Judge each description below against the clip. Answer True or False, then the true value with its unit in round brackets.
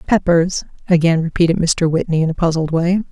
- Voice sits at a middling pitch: True (170 Hz)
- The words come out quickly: False (175 wpm)